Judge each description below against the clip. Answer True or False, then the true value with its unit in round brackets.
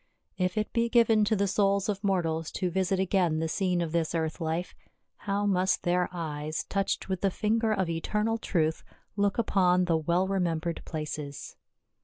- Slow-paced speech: False (175 wpm)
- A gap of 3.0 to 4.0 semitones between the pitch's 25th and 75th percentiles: True (3.4 semitones)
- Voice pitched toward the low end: False (185 Hz)